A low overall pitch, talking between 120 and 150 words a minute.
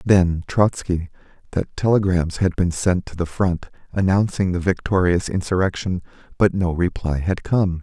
Yes: very low, 90 Hz; average, 145 wpm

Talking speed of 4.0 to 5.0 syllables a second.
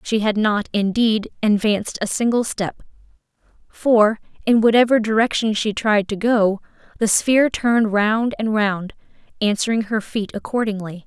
Yes: 4.7 syllables/s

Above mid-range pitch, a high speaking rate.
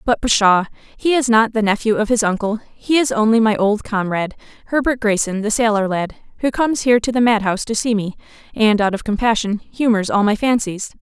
Yes: high, 220 Hz; fast, 210 wpm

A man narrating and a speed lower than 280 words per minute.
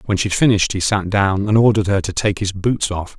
No: male; fast, 285 wpm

